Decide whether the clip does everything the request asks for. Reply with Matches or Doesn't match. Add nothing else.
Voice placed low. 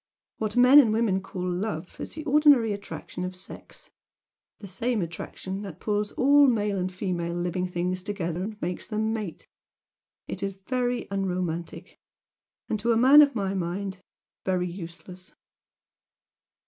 Doesn't match